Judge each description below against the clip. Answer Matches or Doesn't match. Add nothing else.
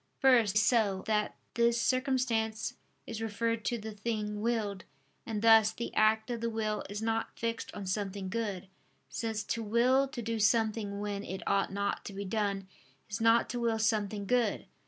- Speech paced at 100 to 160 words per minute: Doesn't match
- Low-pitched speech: Doesn't match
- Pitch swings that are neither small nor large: Doesn't match